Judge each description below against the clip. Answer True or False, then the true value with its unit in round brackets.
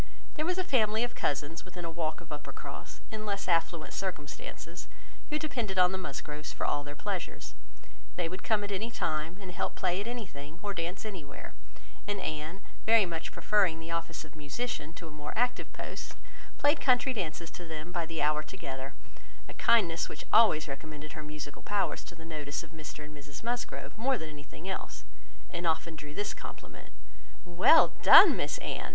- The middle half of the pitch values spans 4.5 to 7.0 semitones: True (5.1 semitones)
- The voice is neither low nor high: True (170 Hz)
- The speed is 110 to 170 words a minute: False (185 wpm)